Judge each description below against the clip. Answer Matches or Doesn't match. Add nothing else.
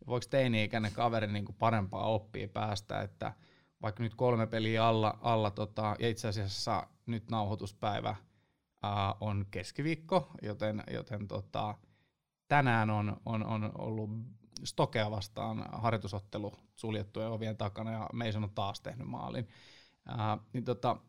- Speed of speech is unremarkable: Matches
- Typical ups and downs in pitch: Doesn't match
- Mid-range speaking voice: Doesn't match